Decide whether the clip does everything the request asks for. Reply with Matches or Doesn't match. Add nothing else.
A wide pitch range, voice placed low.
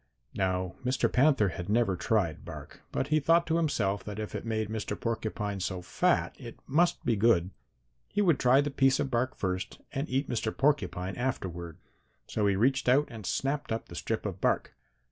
Matches